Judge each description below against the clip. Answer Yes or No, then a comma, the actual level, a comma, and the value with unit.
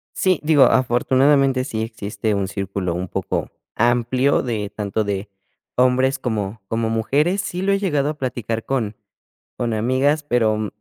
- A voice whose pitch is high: No, low, 120 Hz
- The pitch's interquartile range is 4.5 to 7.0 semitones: No, average, 4.0 semitones